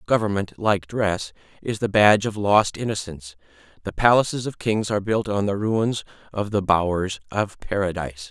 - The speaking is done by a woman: No, male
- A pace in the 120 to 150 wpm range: No, average, 165 wpm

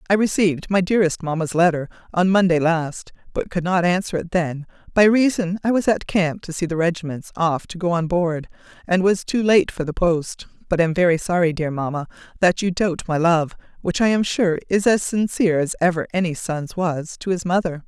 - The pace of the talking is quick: Yes, fast, 210 wpm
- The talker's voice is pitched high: No, medium, 175 Hz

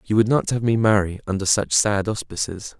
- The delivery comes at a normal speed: No, fast, 215 wpm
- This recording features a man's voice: Yes, male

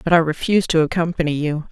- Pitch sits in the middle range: Yes, medium, 160 Hz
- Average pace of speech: No, fast, 210 wpm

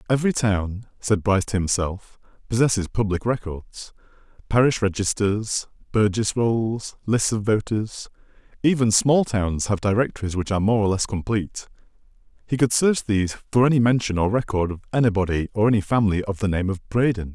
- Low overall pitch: Yes, low, 105 Hz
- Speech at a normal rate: Yes, average, 150 wpm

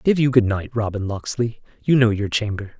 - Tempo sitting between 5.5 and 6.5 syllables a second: No, 5.2 syllables/s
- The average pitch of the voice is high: No, low, 115 Hz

